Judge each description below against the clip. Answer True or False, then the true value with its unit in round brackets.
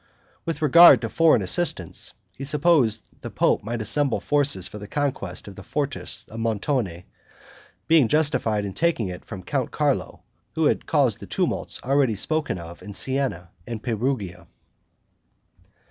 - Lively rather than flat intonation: True (6.3 semitones)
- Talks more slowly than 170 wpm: True (150 wpm)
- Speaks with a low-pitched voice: True (120 Hz)